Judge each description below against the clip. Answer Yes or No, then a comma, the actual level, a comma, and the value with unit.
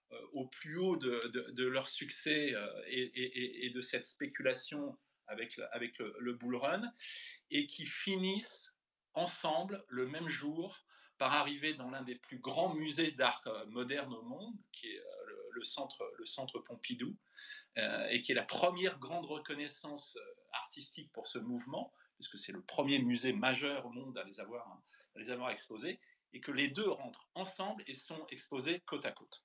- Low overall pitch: No, medium, 155 Hz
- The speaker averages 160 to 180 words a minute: Yes, average, 175 wpm